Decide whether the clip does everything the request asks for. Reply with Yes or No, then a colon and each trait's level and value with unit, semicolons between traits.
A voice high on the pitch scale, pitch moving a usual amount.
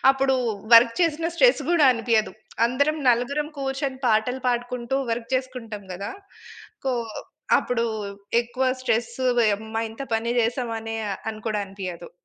Yes: high, 235 Hz; average, 3.1 semitones